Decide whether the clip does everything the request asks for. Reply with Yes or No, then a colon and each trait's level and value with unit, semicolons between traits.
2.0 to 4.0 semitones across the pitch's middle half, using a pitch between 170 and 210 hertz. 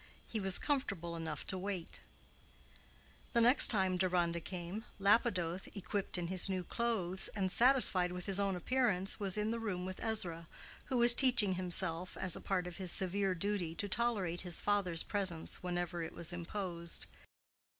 Yes: average, 2.7 semitones; medium, 185 Hz